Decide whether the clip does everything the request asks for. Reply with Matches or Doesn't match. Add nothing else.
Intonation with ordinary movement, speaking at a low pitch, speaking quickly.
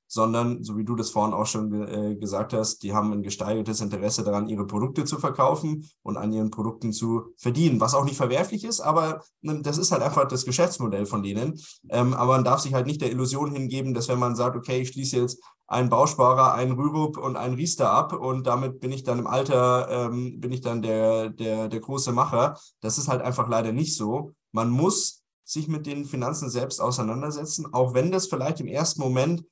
Matches